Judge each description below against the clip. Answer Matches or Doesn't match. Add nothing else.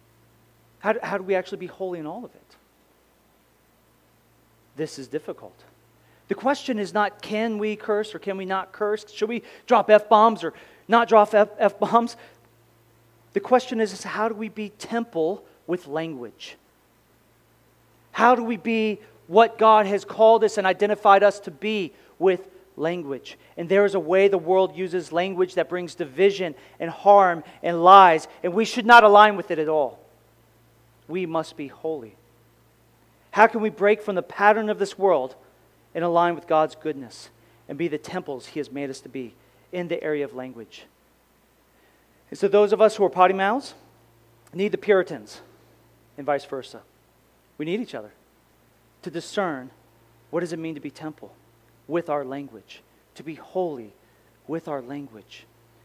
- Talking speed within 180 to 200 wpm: Doesn't match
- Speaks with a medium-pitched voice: Matches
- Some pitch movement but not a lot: Doesn't match